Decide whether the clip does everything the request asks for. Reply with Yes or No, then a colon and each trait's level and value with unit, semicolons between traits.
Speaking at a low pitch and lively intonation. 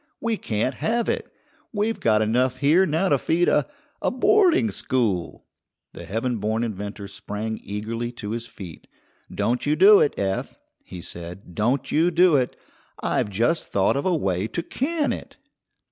Yes: low, 120 Hz; wide, 8.6 semitones